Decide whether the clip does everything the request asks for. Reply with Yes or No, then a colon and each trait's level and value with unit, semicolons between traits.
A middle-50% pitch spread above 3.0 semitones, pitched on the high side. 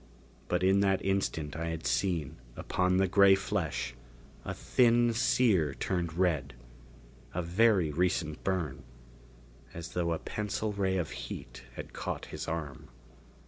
No: average, 3.4 semitones; very low, 90 Hz